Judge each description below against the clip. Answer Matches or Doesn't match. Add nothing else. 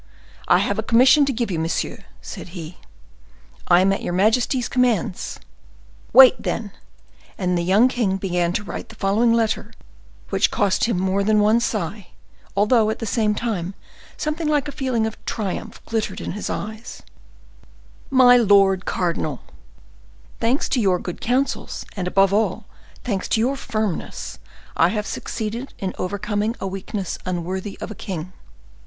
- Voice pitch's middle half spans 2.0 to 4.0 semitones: Matches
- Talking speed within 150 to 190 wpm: Matches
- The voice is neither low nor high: Doesn't match